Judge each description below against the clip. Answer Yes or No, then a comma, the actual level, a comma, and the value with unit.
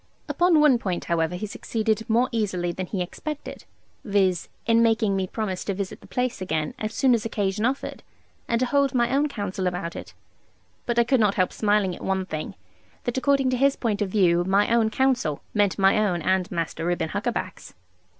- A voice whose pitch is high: Yes, high, 210 Hz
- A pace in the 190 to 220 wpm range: Yes, average, 200 wpm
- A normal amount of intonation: Yes, average, 4.4 semitones